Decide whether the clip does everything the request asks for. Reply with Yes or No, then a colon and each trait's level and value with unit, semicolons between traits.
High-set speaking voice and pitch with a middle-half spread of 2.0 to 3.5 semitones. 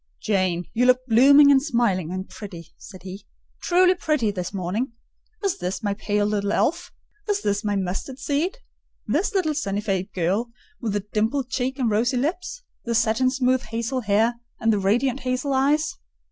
No: high, 235 Hz; average, 5.1 semitones